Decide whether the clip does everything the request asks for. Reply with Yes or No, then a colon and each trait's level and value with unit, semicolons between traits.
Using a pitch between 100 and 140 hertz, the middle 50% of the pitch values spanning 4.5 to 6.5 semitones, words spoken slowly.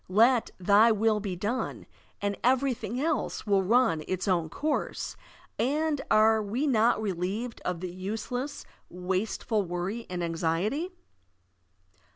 No: high, 215 Hz; average, 5.0 semitones; slow, 125 wpm